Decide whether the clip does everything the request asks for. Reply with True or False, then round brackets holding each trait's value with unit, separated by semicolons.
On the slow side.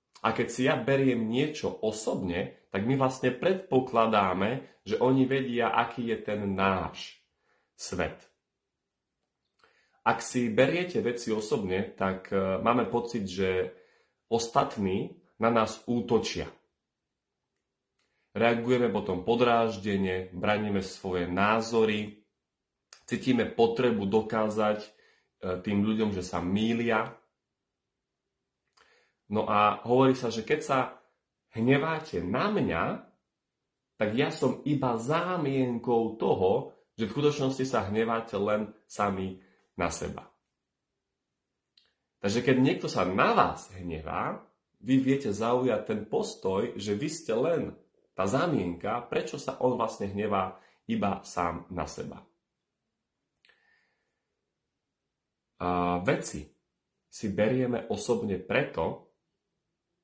True (105 wpm)